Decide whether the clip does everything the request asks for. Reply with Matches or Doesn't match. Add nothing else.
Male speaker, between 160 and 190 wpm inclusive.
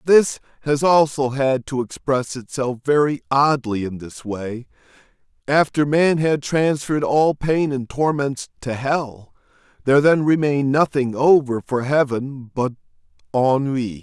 Doesn't match